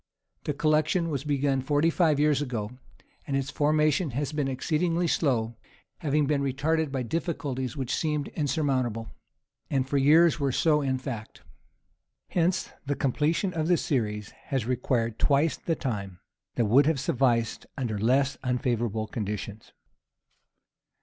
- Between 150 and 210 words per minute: No, average, 140 wpm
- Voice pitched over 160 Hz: No, medium, 140 Hz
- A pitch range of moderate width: Yes, average, 3.7 semitones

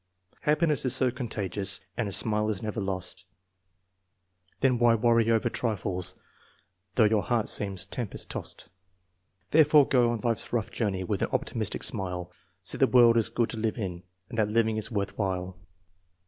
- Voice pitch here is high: No, low, 110 Hz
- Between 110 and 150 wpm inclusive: No, average, 170 wpm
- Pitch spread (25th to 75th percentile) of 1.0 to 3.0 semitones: No, average, 3.4 semitones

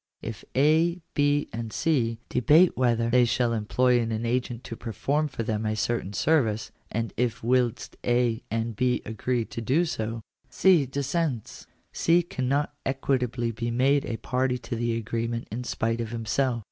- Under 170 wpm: Yes, average, 160 wpm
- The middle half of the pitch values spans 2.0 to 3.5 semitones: Yes, average, 2.9 semitones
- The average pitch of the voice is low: Yes, low, 120 Hz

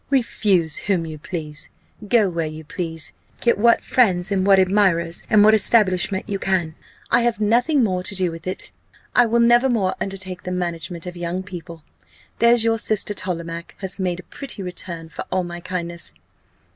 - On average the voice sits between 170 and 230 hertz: Yes, medium, 185 Hz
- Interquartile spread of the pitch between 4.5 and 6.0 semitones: No, average, 3.7 semitones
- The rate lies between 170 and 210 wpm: Yes, average, 180 wpm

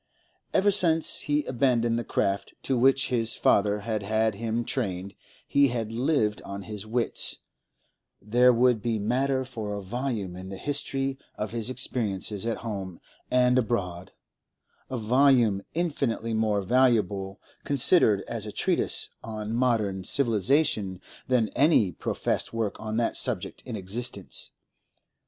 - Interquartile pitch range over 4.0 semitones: No, average, 3.7 semitones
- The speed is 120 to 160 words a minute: Yes, average, 140 wpm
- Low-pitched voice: Yes, low, 115 Hz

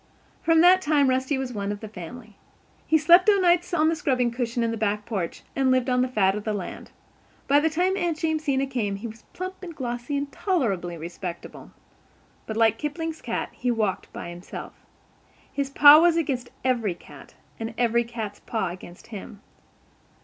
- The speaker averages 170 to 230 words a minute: Yes, average, 185 wpm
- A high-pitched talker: Yes, very high, 250 Hz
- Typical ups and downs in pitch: No, wide, 6.3 semitones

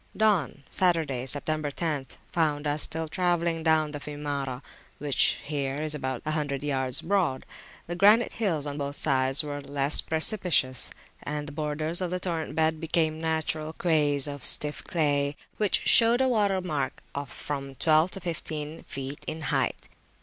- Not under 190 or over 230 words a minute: No, average, 160 wpm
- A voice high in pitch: No, medium, 155 Hz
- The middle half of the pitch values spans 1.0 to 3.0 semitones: Yes, narrow, 2.6 semitones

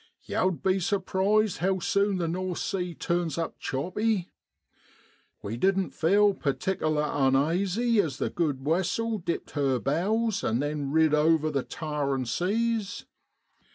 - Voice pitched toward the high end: No, medium, 175 Hz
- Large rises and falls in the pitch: No, average, 4.7 semitones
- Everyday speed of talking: No, slow, 130 wpm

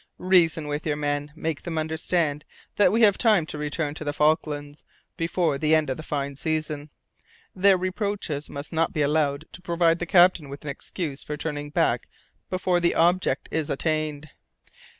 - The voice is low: No, medium, 155 Hz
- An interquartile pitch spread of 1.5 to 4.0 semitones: Yes, average, 2.9 semitones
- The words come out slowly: No, average, 175 wpm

